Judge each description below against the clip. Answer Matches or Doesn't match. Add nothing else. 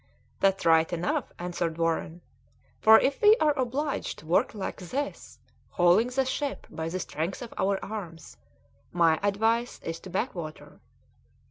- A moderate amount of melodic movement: Doesn't match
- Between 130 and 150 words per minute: Matches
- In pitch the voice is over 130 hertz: Matches